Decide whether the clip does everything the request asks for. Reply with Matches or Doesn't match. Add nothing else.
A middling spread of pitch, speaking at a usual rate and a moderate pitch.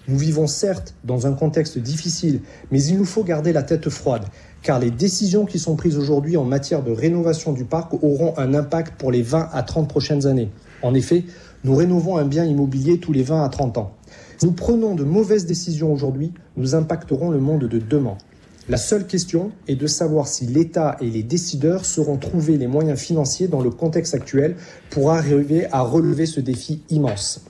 Matches